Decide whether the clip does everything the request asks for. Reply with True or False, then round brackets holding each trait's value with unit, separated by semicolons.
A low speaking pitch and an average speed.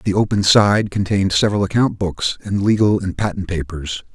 True (100 Hz; 175 wpm)